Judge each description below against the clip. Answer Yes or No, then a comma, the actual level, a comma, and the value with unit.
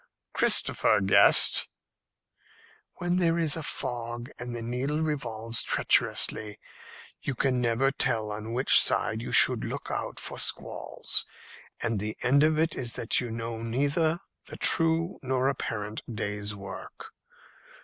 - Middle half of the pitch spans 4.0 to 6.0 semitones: Yes, average, 4.3 semitones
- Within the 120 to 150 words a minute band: Yes, average, 140 wpm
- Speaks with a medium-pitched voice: No, low, 120 Hz